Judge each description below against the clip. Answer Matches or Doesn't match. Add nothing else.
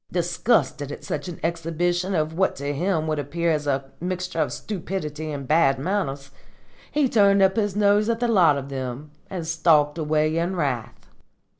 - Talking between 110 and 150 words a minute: Doesn't match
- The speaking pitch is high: Doesn't match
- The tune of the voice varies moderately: Matches